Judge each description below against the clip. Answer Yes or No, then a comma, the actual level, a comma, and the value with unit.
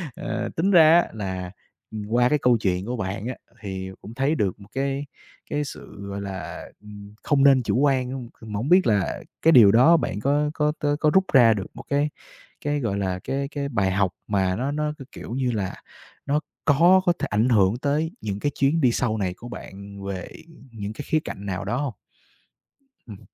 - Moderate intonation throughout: No, wide, 6.2 semitones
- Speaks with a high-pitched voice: No, low, 120 Hz